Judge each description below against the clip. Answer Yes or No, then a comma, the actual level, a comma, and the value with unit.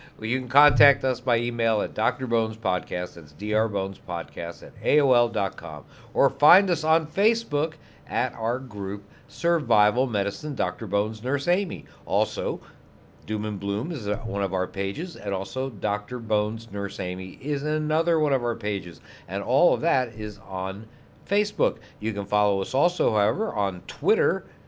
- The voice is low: Yes, low, 110 Hz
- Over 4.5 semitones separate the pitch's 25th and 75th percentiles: Yes, average, 5.2 semitones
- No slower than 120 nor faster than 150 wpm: No, average, 160 wpm